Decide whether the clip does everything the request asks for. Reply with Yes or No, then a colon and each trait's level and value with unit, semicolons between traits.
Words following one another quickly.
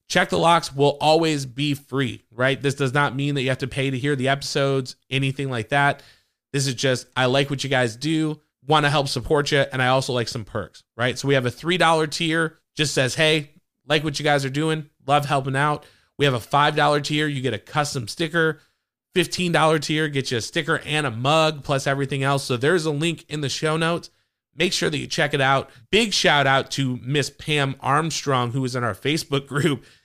Yes: fast, 230 wpm